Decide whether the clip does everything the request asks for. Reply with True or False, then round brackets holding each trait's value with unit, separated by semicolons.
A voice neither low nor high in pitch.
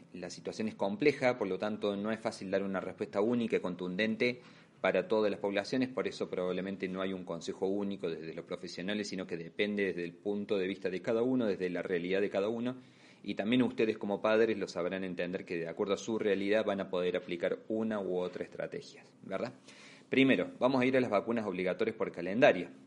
False (100 Hz)